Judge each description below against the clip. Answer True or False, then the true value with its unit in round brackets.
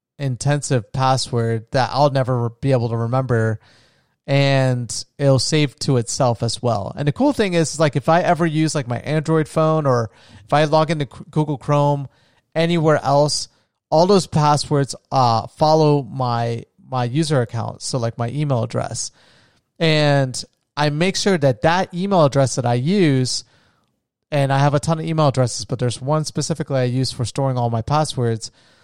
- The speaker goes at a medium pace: True (175 wpm)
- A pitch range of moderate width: True (4.1 semitones)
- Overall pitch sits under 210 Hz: True (140 Hz)